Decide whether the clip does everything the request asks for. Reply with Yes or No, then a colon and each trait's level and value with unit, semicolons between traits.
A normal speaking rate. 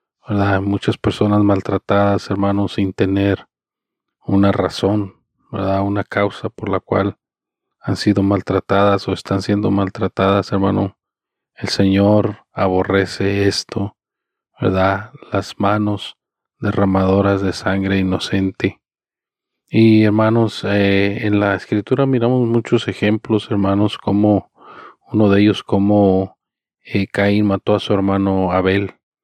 No: slow, 115 wpm